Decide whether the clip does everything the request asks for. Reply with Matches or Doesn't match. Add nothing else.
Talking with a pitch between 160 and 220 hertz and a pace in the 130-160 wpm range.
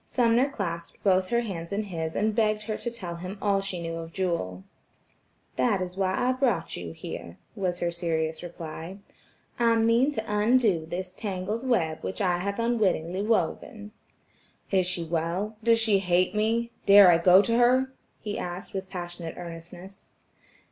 Doesn't match